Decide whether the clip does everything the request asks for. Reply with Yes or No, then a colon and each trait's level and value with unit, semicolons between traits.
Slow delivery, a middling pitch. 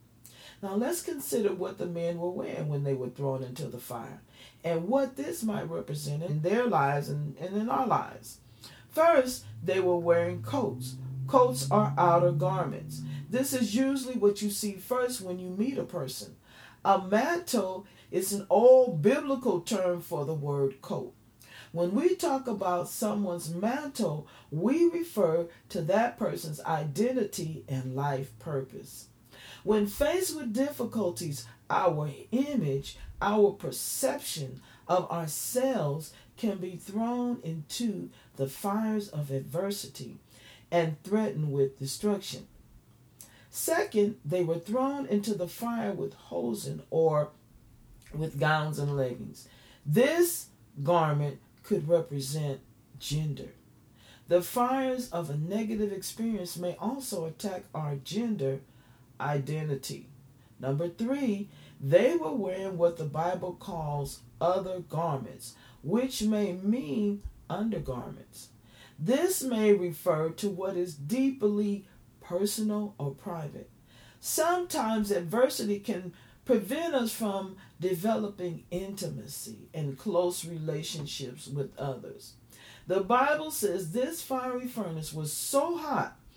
Yes: slow, 120 wpm; medium, 175 Hz